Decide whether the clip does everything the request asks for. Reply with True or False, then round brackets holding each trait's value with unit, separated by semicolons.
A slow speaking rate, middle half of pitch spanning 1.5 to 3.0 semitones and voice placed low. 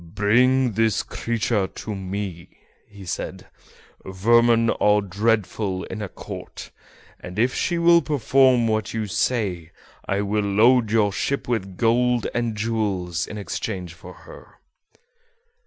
False (130 wpm; 3.4 semitones; 105 Hz)